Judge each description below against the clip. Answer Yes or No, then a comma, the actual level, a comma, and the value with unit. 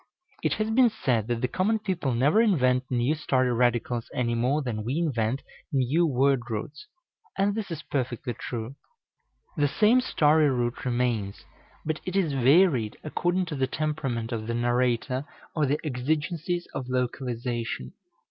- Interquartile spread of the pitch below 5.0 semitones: Yes, average, 4.6 semitones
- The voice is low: Yes, low, 130 Hz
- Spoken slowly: No, average, 155 wpm